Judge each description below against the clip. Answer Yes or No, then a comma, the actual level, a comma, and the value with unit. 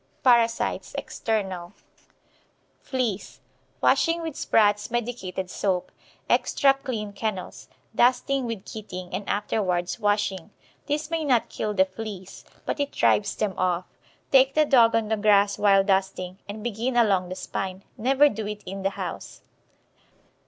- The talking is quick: No, average, 140 wpm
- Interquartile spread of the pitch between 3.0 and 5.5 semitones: Yes, average, 3.9 semitones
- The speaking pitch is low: No, high, 210 Hz